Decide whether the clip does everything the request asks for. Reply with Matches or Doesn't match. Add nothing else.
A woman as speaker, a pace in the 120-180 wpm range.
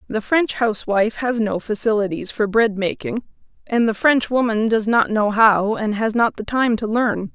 Doesn't match